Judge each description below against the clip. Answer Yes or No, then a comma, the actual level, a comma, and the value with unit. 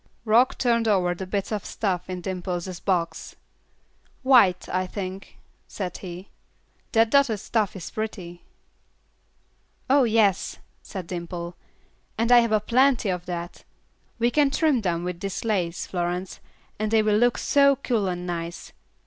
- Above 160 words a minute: No, average, 145 wpm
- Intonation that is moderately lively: Yes, average, 4.3 semitones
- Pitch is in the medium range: No, high, 195 Hz